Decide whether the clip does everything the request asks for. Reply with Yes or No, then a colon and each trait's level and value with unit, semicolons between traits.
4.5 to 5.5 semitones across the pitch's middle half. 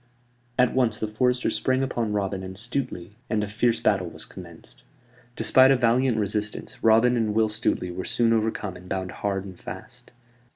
No: average, 3.6 semitones